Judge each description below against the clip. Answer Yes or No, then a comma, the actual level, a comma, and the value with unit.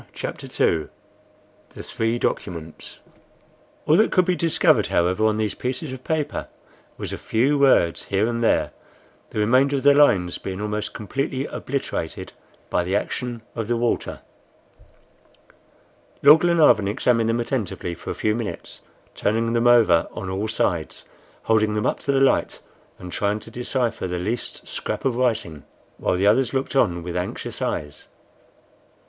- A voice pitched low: Yes, low, 115 Hz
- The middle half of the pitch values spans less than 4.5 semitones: No, average, 5.1 semitones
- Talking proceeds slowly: No, average, 155 wpm